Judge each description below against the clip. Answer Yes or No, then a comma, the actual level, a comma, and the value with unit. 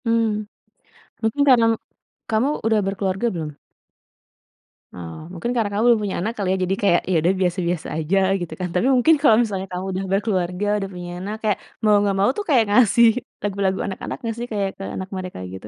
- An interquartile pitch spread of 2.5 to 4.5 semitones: Yes, average, 3.4 semitones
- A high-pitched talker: Yes, high, 195 Hz